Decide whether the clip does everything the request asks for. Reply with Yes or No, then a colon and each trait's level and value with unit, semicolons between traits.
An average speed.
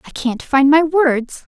Yes: average, 195 wpm